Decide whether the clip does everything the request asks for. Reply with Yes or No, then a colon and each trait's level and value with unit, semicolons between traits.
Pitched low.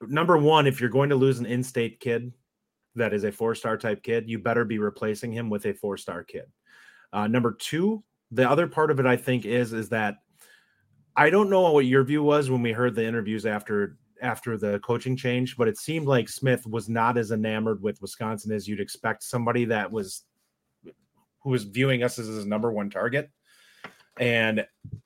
Yes: low, 120 Hz